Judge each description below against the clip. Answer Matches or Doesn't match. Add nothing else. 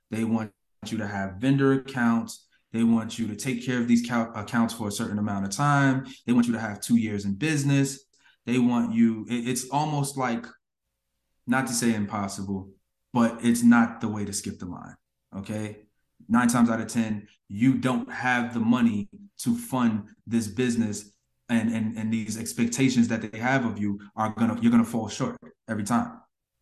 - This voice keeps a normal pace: Matches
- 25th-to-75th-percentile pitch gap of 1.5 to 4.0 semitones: Matches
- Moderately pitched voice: Doesn't match